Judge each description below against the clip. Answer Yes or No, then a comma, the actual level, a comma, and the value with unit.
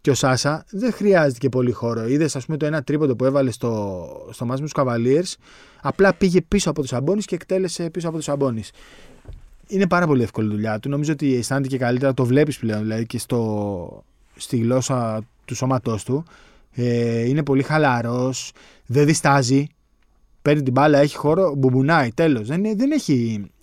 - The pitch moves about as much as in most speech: Yes, average, 4.3 semitones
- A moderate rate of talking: No, fast, 175 wpm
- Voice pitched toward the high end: No, low, 135 Hz